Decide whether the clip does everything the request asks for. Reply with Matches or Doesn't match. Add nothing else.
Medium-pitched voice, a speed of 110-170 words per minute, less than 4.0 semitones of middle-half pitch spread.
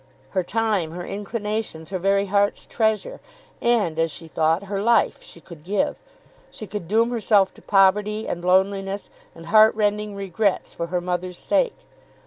Doesn't match